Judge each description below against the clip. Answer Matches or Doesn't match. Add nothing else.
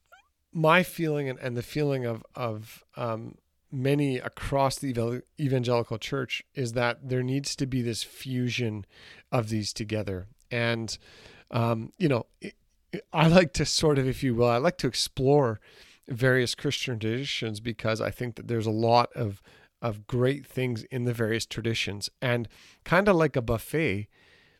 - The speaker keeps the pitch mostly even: Doesn't match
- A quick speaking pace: Doesn't match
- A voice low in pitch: Matches